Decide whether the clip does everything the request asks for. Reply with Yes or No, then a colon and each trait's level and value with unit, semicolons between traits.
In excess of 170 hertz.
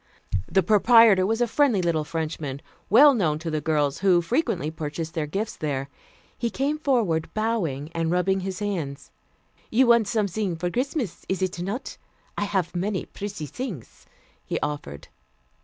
Yes: medium, 185 Hz